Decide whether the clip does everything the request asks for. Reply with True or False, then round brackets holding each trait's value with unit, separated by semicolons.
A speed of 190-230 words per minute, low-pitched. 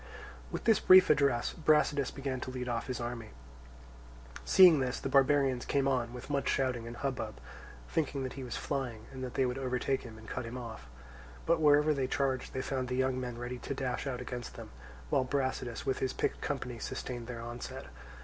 True (200 wpm; 130 Hz)